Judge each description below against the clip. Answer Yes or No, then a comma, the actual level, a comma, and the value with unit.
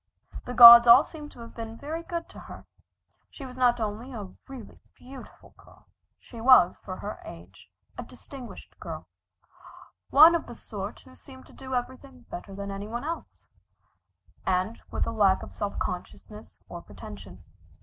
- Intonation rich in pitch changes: No, average, 4.0 semitones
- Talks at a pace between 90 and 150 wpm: No, average, 170 wpm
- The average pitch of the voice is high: Yes, high, 240 Hz